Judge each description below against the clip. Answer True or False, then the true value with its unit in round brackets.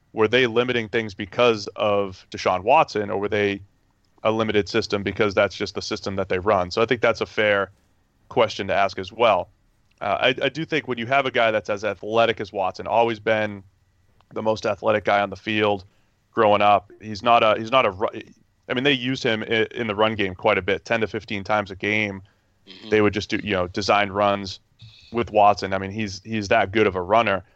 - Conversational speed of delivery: False (220 wpm)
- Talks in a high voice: False (105 Hz)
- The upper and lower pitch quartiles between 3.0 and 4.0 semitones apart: False (2.4 semitones)